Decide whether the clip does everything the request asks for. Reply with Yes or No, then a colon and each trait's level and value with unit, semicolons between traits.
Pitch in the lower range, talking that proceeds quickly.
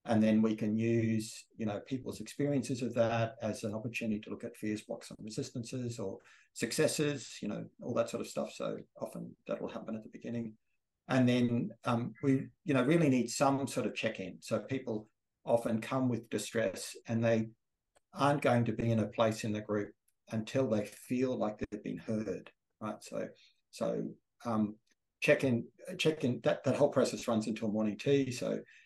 No: low, 115 Hz; average, 185 wpm